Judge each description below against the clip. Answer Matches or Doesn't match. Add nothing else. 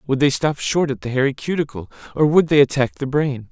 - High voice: Doesn't match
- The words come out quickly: Matches